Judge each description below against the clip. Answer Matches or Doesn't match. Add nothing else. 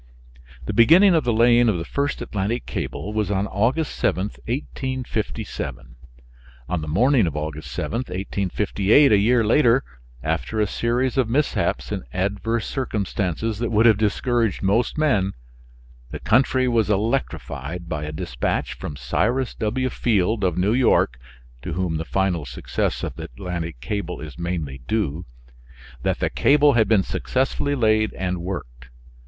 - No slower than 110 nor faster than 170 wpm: Matches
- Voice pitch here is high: Doesn't match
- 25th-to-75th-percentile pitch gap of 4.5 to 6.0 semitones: Matches